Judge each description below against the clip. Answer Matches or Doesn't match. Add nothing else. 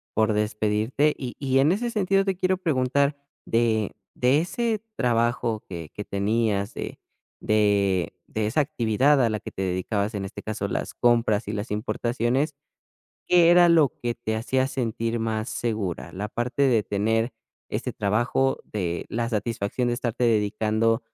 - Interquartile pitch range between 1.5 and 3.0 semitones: Doesn't match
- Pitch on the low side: Matches